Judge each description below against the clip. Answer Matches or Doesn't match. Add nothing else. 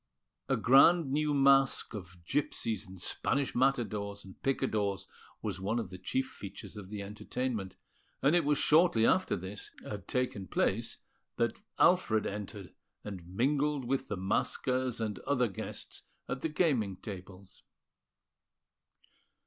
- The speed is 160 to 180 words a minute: Doesn't match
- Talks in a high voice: Doesn't match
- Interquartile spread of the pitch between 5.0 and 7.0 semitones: Matches